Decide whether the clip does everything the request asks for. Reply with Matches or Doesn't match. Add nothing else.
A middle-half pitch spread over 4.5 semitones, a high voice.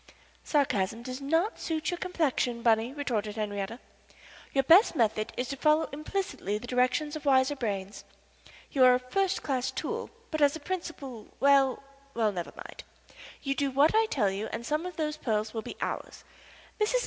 Matches